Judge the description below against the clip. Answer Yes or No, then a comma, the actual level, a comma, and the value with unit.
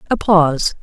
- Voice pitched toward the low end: No, medium, 170 Hz